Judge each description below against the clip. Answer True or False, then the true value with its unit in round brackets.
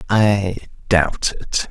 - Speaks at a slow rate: True (105 wpm)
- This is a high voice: False (100 Hz)